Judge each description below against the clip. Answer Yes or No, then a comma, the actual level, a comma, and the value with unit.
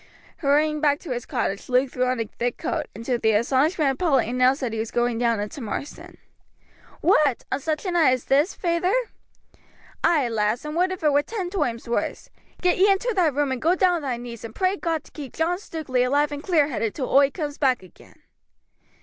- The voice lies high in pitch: Yes, very high, 280 Hz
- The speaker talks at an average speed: No, fast, 220 wpm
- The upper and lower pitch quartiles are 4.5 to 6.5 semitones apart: Yes, average, 5.1 semitones